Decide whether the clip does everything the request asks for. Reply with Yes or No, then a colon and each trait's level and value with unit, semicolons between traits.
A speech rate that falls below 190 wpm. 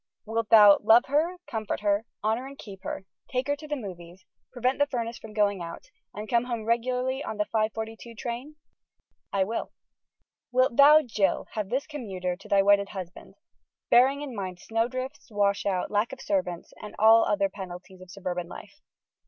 Yes: average, 175 wpm